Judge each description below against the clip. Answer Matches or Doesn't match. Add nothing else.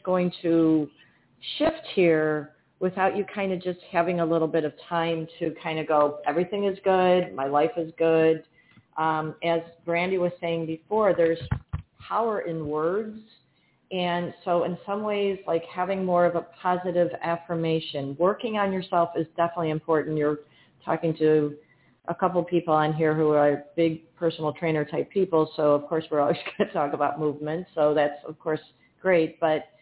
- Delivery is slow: Doesn't match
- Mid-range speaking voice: Matches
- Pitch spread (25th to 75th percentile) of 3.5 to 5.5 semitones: Doesn't match